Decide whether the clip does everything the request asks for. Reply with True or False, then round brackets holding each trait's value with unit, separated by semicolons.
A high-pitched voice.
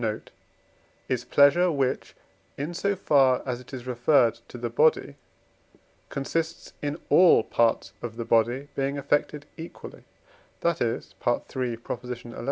False (135 Hz)